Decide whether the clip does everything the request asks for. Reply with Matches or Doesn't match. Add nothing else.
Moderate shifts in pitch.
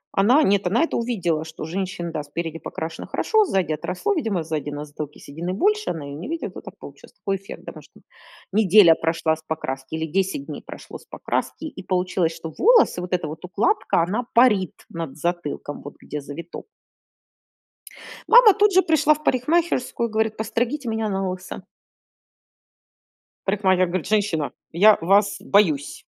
Doesn't match